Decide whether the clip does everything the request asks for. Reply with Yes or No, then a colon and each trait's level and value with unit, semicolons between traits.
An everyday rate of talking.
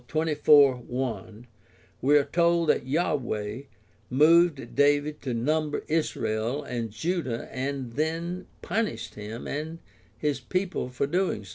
No: slow, 120 wpm